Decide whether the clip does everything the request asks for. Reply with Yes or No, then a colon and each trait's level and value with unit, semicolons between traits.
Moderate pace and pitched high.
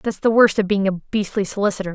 No: fast, 245 wpm; high, 200 Hz